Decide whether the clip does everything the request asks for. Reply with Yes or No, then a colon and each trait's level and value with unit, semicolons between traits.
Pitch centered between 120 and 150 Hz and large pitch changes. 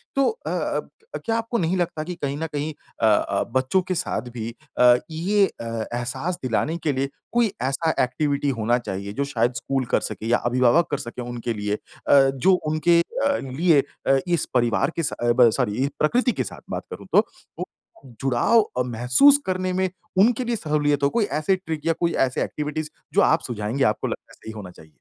Yes: medium, 140 Hz; wide, 6.2 semitones